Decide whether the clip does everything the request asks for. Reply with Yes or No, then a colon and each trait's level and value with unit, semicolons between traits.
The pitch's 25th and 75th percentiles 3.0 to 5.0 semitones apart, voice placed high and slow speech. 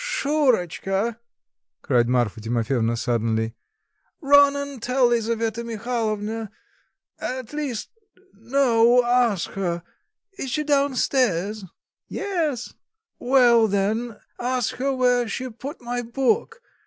Yes: average, 4.5 semitones; high, 235 Hz; slow, 105 wpm